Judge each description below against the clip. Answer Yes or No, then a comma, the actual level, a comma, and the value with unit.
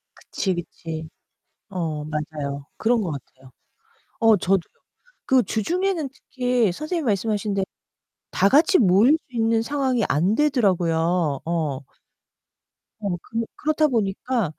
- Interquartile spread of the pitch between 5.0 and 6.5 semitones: No, wide, 7.2 semitones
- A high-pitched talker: Yes, high, 205 Hz